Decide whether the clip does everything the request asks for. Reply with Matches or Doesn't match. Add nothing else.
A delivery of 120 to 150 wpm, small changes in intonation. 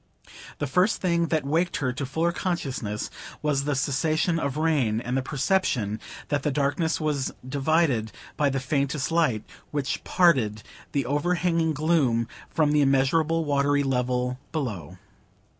Doesn't match